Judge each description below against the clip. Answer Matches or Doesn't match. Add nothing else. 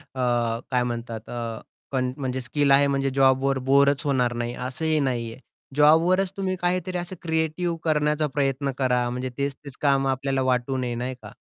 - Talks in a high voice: Doesn't match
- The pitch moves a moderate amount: Matches